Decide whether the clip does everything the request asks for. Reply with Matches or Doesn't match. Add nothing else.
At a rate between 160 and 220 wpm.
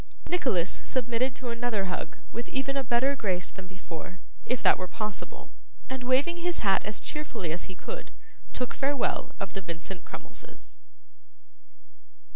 Doesn't match